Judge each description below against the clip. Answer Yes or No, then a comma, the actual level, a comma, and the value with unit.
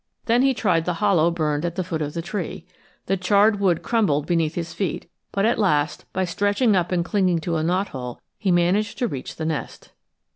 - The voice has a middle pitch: Yes, medium, 175 Hz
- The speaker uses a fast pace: Yes, fast, 210 wpm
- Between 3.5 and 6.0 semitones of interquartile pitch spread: Yes, average, 3.9 semitones